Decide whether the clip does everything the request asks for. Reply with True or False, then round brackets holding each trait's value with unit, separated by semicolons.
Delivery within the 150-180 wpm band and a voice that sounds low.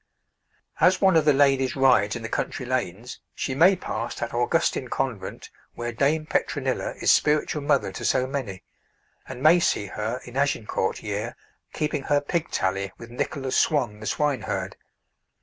True (160 wpm; 130 Hz)